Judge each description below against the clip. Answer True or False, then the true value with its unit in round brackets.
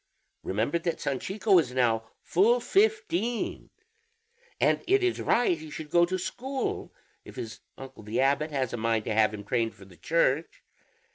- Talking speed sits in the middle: True (165 wpm)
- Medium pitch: True (150 Hz)